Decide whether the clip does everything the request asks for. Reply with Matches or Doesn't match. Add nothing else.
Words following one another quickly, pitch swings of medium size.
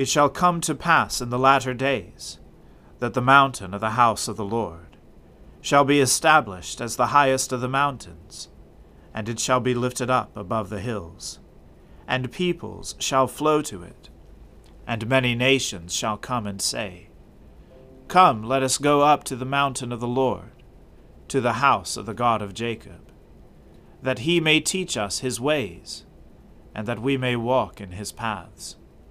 Doesn't match